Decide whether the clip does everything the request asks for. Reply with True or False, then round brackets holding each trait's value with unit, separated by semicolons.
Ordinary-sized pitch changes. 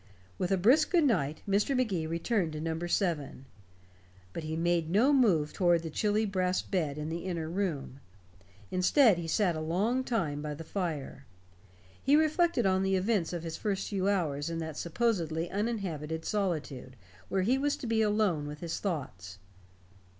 True (4.8 semitones)